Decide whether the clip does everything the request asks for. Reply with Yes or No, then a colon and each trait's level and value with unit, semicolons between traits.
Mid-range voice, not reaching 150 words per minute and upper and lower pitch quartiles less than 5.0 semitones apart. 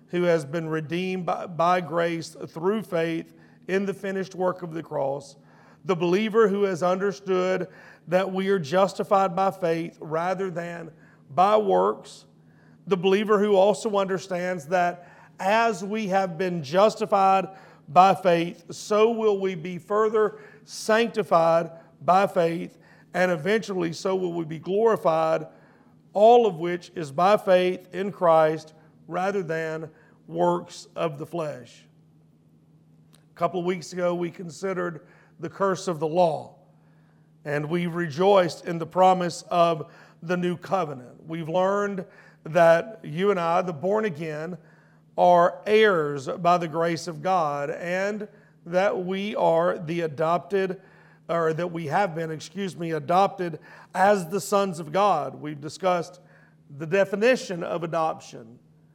Yes: medium, 175 Hz; average, 140 wpm; average, 2.8 semitones